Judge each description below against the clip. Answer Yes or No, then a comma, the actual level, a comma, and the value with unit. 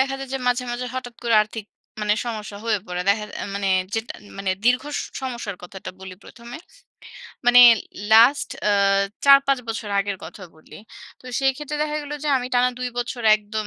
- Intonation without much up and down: No, average, 3.7 semitones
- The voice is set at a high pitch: Yes, high, 240 Hz